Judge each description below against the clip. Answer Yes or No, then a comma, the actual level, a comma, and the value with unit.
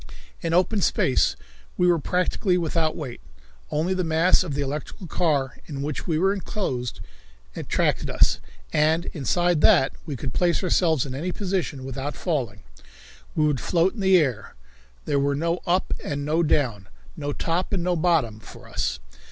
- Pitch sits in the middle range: Yes, medium, 160 Hz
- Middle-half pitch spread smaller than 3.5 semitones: No, average, 4.2 semitones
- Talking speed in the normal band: Yes, average, 170 wpm